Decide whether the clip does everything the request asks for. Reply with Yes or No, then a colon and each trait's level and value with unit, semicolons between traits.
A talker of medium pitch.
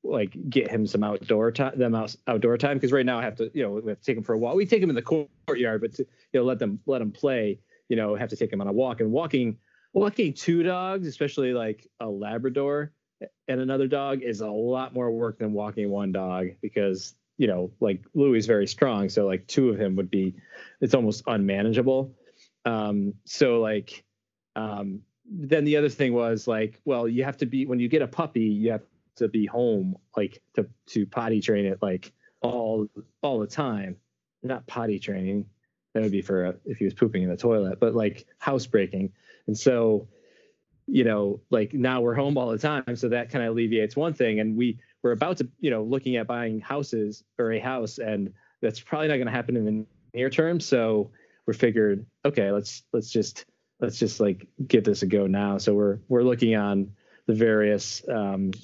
No: low, 115 Hz